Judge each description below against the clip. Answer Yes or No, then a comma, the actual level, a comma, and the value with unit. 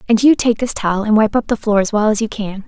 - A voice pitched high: Yes, high, 215 Hz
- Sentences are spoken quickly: Yes, fast, 335 wpm